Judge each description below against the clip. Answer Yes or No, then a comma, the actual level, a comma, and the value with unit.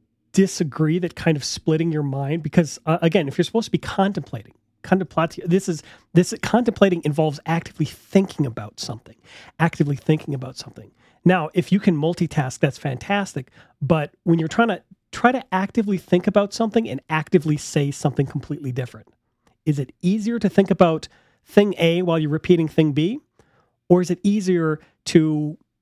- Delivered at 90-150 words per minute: No, average, 165 wpm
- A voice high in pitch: No, medium, 165 Hz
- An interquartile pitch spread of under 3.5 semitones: No, average, 4.0 semitones